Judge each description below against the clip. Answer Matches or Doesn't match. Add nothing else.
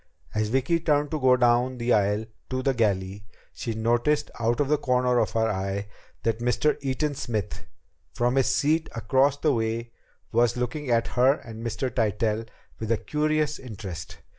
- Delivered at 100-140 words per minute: Doesn't match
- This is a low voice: Matches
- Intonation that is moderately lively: Matches